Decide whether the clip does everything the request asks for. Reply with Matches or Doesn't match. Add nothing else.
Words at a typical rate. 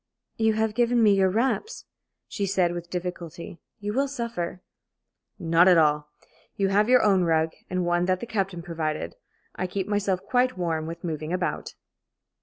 Matches